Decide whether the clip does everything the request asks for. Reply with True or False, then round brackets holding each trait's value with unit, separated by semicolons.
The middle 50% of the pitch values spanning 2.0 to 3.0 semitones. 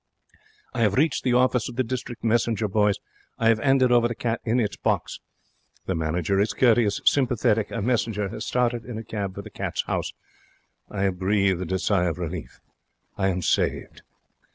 False (3.8 semitones)